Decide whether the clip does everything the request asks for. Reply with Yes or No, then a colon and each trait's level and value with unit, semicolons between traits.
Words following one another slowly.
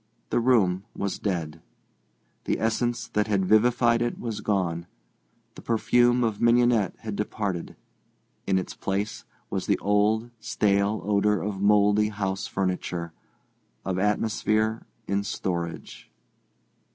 Yes: slow, 120 wpm